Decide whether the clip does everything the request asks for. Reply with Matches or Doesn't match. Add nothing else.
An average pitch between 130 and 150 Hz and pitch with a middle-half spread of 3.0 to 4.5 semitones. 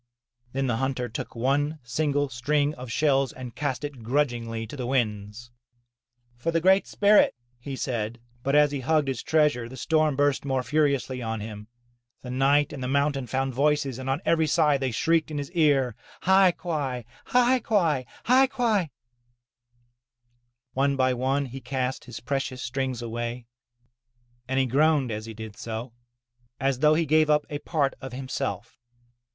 Matches